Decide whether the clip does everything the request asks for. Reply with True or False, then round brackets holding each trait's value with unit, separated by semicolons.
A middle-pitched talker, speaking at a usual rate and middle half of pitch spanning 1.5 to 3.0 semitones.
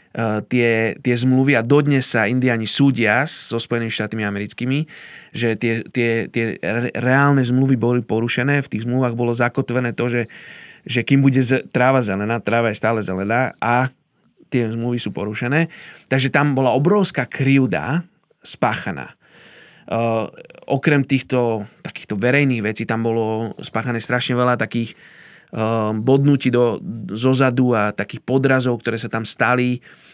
False (120 Hz; 140 wpm; 2.7 semitones)